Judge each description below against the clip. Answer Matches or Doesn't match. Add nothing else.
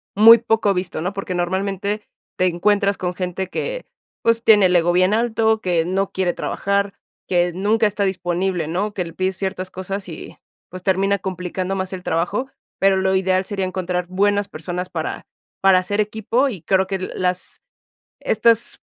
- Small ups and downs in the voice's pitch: Matches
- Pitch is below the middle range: Doesn't match